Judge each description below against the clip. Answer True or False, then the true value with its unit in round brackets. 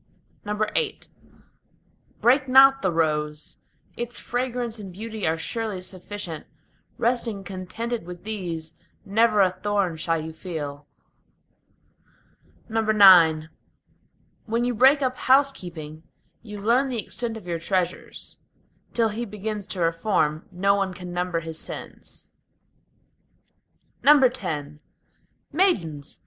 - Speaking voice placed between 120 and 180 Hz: False (200 Hz)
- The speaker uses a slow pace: True (110 wpm)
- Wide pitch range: True (5.8 semitones)